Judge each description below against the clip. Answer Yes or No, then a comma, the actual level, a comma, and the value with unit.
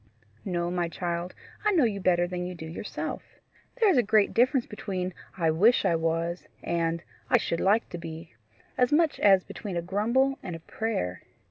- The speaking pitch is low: No, medium, 180 Hz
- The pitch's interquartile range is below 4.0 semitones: No, average, 4.9 semitones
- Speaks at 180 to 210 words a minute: Yes, average, 190 wpm